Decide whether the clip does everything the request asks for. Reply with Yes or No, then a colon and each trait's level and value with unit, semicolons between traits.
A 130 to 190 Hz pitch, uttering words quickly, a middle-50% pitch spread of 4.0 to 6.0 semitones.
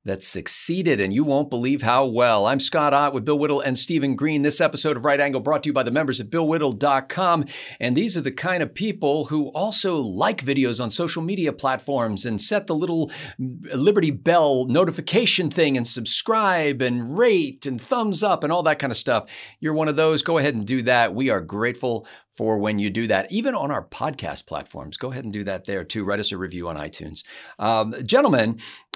Yes: medium, 140 Hz; fast, 215 wpm; average, 5.1 semitones